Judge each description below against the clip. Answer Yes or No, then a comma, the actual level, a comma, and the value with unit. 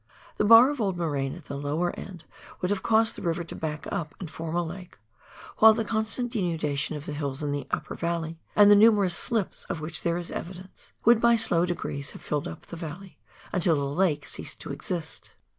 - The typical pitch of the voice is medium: Yes, medium, 175 Hz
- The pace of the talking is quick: Yes, fast, 220 wpm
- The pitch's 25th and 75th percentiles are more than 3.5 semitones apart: Yes, average, 4.9 semitones